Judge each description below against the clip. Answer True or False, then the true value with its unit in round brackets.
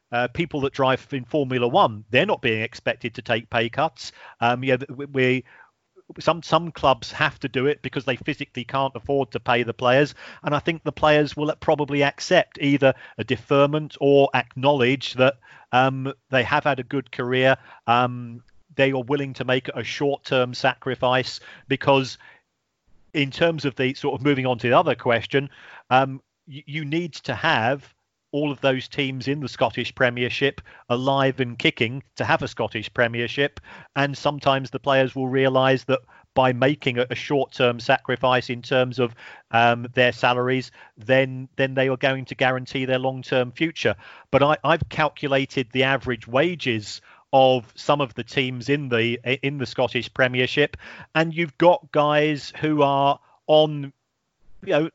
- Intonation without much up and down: True (2.3 semitones)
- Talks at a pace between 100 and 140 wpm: False (170 wpm)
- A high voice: False (135 Hz)